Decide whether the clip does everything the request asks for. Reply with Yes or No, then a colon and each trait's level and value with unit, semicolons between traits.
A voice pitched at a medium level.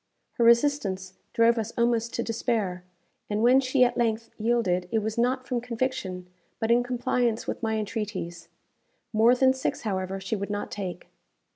No: high, 230 Hz